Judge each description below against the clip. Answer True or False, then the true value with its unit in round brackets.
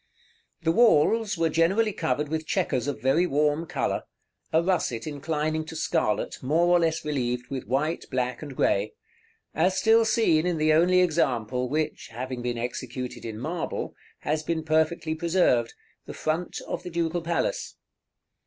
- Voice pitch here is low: False (155 Hz)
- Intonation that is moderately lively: True (4.8 semitones)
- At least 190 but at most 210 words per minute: False (160 wpm)